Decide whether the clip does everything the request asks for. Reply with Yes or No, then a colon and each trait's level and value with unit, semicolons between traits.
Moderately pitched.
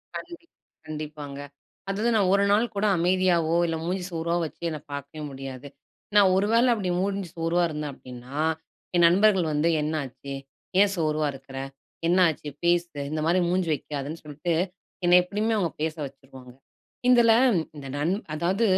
Yes: medium, 165 Hz